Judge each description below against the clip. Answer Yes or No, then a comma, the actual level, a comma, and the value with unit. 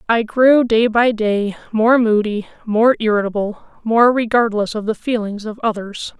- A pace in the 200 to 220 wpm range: No, average, 155 wpm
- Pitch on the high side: Yes, high, 220 Hz